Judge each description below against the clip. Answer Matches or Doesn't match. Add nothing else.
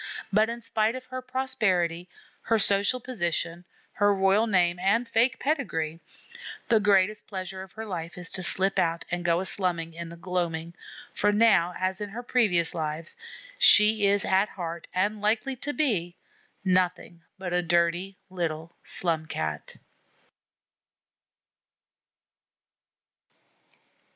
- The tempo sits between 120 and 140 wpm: Matches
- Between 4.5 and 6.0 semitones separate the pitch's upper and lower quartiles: Doesn't match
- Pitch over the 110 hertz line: Matches